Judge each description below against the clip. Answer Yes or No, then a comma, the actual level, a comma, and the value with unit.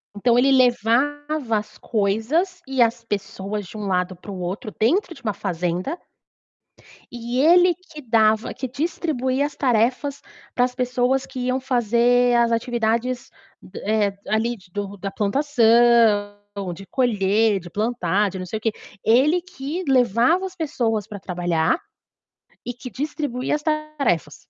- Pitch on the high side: Yes, high, 235 Hz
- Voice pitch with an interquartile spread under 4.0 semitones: No, average, 4.4 semitones